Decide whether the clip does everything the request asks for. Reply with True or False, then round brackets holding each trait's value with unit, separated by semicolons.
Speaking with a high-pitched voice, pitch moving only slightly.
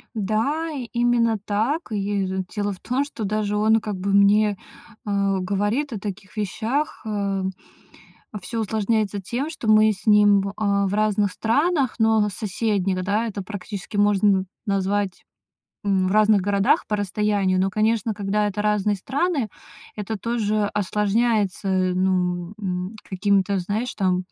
True (205 Hz; 2.0 semitones)